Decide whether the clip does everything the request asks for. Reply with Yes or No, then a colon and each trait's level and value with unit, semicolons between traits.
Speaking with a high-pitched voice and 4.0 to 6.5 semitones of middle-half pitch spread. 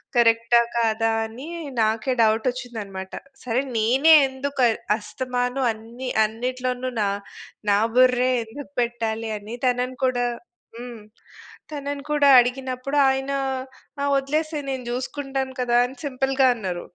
No: very high, 250 Hz; average, 2.8 semitones